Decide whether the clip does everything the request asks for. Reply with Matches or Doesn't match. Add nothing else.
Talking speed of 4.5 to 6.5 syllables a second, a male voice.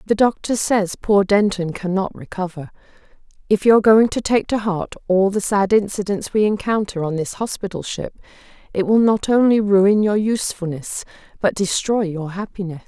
Doesn't match